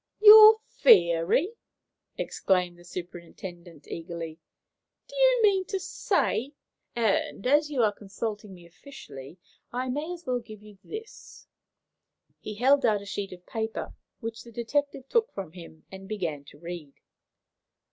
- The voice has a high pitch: Yes, high, 215 Hz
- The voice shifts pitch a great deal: Yes, wide, 8.5 semitones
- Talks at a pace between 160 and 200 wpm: No, average, 145 wpm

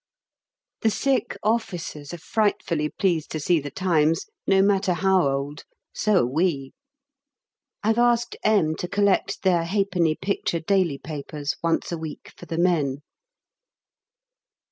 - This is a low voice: No, medium, 175 Hz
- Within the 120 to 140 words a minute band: Yes, slow, 135 wpm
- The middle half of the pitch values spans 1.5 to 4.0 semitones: No, average, 4.4 semitones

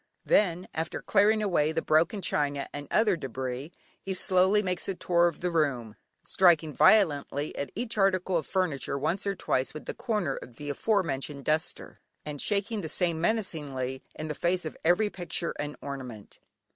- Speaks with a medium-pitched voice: Yes, medium, 165 Hz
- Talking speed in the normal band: Yes, average, 175 wpm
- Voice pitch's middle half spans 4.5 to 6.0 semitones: Yes, average, 4.9 semitones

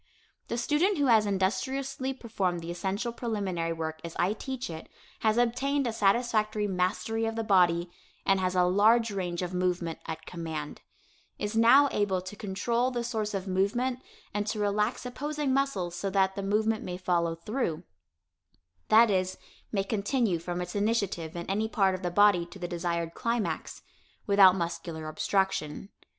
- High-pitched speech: Yes, high, 200 Hz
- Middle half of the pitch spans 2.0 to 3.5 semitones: No, average, 4.4 semitones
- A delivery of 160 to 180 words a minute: Yes, average, 165 wpm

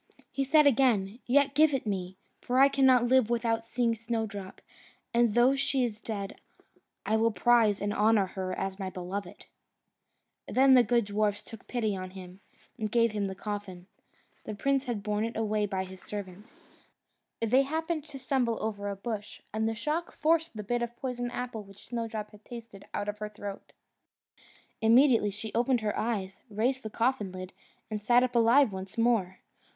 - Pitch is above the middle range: Yes, high, 225 Hz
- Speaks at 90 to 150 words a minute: No, average, 180 wpm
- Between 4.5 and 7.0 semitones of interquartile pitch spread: No, average, 3.2 semitones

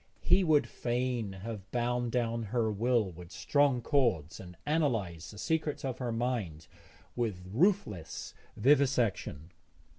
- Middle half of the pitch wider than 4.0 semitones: Yes, average, 4.9 semitones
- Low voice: Yes, low, 120 Hz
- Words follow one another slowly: Yes, slow, 125 wpm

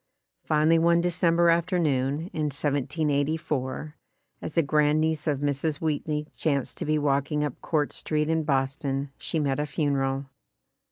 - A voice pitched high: No, medium, 150 Hz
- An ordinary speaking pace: Yes, average, 145 wpm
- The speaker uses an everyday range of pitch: No, narrow, 2.2 semitones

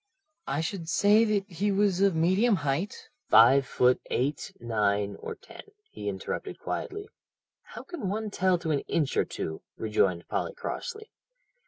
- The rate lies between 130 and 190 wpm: Yes, average, 160 wpm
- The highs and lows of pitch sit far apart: Yes, wide, 8.1 semitones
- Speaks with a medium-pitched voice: Yes, medium, 175 Hz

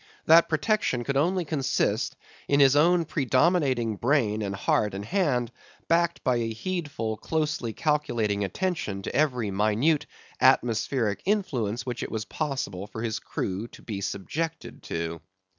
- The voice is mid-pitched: No, low, 125 Hz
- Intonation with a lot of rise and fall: Yes, wide, 6.3 semitones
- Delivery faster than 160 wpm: No, average, 140 wpm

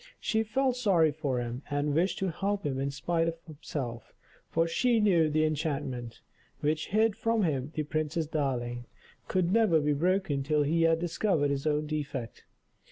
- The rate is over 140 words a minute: Yes, average, 170 wpm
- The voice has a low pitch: No, medium, 155 Hz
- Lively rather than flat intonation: No, average, 4.1 semitones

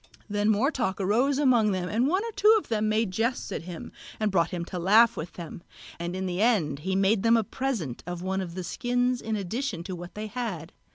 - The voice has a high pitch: Yes, high, 205 Hz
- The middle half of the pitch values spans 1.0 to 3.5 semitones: No, average, 4.9 semitones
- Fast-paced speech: Yes, fast, 235 wpm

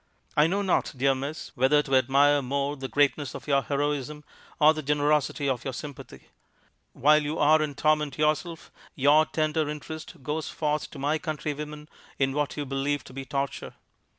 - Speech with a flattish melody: Yes, narrow, 1.7 semitones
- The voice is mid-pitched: Yes, medium, 145 Hz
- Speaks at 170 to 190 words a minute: Yes, average, 175 wpm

